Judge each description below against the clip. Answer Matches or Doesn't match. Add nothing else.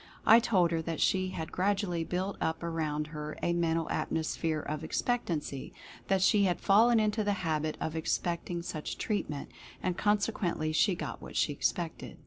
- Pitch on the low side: Doesn't match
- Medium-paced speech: Matches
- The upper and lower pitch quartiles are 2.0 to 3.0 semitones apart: Doesn't match